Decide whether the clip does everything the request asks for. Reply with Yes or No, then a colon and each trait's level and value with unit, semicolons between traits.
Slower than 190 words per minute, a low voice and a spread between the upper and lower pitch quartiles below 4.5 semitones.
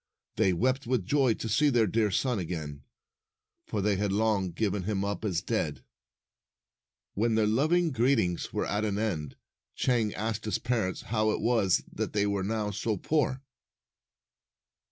Yes: average, 160 wpm; low, 110 Hz; average, 3.3 semitones